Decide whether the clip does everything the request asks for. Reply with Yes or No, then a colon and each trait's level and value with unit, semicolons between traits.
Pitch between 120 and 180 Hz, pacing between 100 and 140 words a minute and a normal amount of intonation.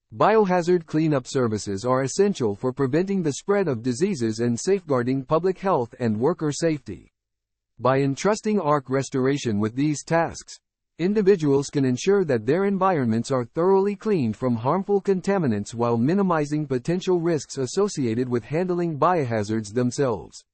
No: medium, 140 Hz; slow, 135 wpm; wide, 6.8 semitones